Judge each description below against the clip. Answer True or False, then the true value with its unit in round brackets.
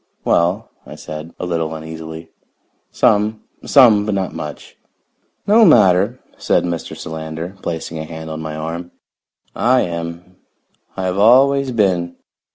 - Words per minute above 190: False (135 wpm)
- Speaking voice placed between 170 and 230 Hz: False (85 Hz)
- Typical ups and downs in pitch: True (4.6 semitones)